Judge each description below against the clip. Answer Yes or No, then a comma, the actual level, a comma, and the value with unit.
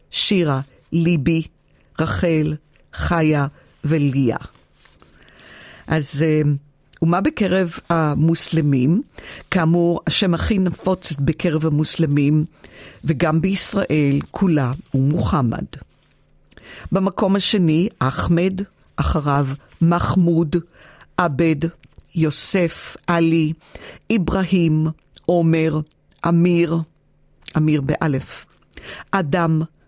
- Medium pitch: Yes, medium, 165 Hz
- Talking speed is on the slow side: Yes, slow, 70 wpm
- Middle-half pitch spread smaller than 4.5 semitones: Yes, narrow, 2.4 semitones